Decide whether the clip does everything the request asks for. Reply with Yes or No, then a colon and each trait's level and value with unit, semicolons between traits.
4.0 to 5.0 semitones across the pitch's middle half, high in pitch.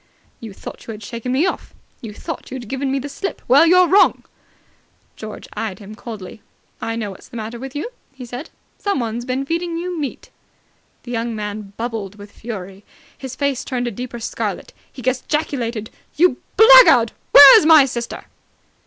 Yes: average, 4.3 semitones; high, 245 Hz